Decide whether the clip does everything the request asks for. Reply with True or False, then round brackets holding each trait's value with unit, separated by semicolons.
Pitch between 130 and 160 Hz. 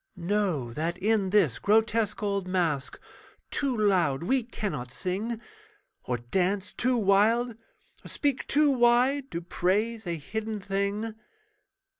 False (205 Hz)